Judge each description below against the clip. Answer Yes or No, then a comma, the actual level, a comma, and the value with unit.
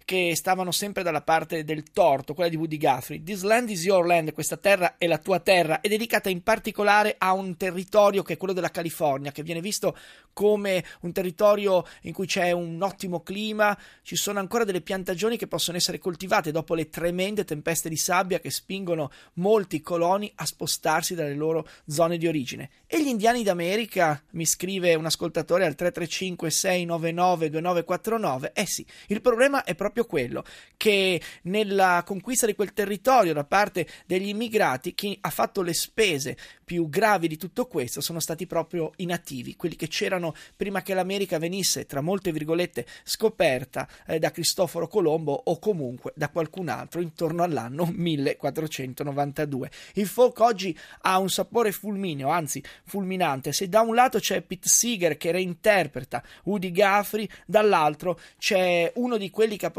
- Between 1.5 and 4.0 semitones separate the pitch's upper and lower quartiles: Yes, average, 3.4 semitones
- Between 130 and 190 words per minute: Yes, average, 165 wpm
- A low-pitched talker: No, medium, 180 Hz